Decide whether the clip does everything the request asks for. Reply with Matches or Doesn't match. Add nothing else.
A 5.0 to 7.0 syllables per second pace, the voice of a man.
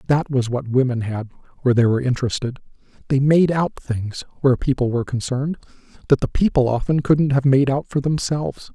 Matches